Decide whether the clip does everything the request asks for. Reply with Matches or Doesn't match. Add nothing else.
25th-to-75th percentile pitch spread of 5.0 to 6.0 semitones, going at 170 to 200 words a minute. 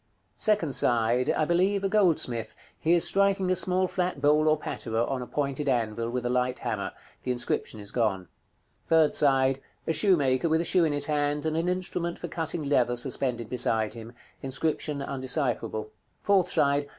Matches